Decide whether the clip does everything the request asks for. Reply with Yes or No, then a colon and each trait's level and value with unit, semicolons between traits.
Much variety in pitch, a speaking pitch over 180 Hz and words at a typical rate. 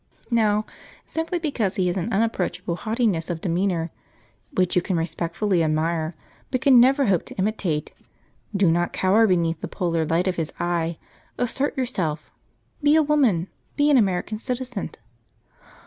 Yes: wide, 5.9 semitones; high, 190 Hz; average, 150 wpm